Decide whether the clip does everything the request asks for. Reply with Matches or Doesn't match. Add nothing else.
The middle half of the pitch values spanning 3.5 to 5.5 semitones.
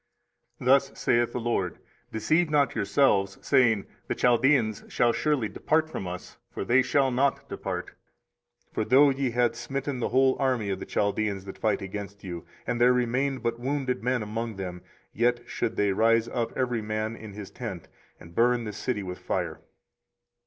Matches